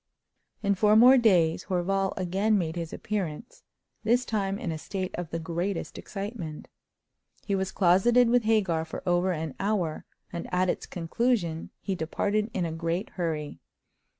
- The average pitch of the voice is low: No, medium, 185 Hz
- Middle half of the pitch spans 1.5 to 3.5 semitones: No, average, 4.0 semitones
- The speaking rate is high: No, average, 155 wpm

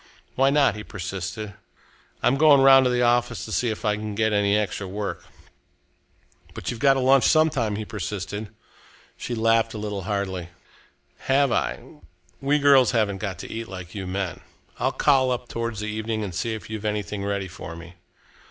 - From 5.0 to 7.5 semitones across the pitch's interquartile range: No, average, 3.7 semitones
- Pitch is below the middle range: Yes, low, 110 Hz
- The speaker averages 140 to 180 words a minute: No, average, 190 wpm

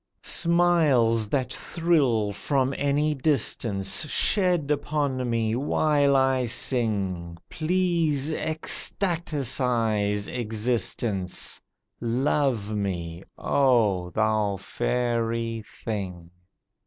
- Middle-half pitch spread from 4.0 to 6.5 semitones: Yes, wide, 5.5 semitones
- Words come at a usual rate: No, slow, 75 wpm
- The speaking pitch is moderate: No, low, 125 Hz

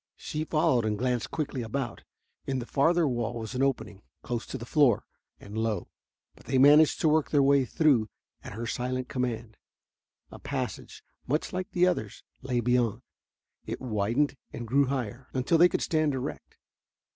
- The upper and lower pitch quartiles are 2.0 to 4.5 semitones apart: Yes, average, 3.9 semitones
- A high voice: No, low, 130 Hz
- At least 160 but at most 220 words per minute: Yes, average, 170 wpm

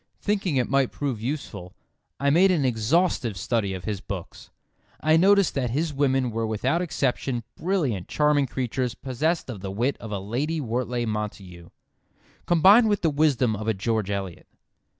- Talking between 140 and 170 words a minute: Yes, average, 165 wpm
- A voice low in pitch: Yes, low, 125 Hz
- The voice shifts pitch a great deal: Yes, wide, 5.9 semitones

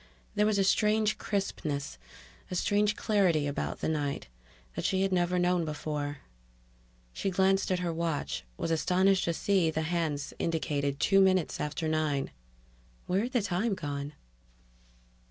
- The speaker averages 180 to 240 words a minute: No, average, 155 wpm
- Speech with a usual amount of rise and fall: Yes, average, 4.4 semitones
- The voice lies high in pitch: No, medium, 175 Hz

